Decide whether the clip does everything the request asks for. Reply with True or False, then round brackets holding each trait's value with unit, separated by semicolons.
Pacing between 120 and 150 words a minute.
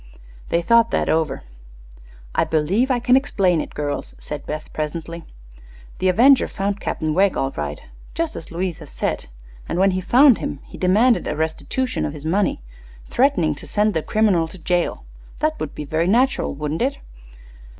False (175 wpm)